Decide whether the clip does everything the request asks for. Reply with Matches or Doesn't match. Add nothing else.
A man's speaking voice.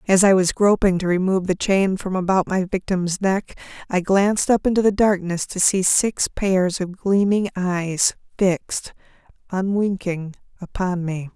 Doesn't match